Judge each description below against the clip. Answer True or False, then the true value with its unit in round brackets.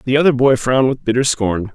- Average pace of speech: False (240 wpm)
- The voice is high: False (125 Hz)